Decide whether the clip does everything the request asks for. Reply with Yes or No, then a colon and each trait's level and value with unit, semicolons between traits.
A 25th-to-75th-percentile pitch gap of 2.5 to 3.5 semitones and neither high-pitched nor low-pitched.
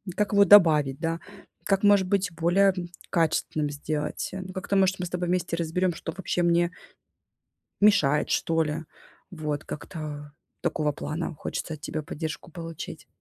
Yes: average, 3.2 semitones; medium, 170 Hz